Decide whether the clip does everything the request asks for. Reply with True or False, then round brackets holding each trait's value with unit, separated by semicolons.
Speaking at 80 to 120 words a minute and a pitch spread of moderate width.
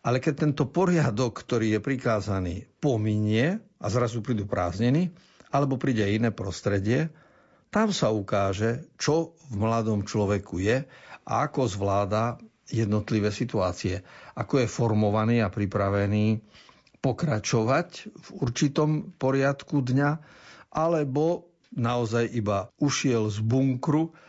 False (115 wpm; 5.8 semitones)